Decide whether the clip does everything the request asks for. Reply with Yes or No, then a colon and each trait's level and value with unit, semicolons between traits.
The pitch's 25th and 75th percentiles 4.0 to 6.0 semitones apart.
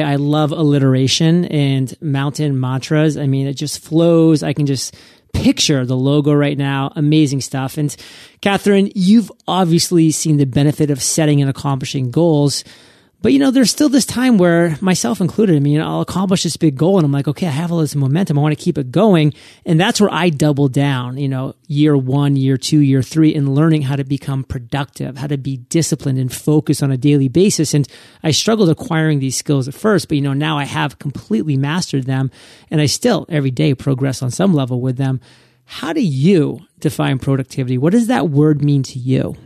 No: average, 3.2 semitones